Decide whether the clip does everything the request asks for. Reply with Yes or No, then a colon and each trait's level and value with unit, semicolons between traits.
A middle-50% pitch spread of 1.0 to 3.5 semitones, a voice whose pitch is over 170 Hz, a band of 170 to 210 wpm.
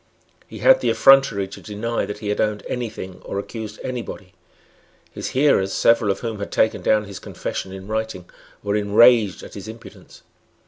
No: narrow, 2.6 semitones; low, 105 Hz; average, 185 wpm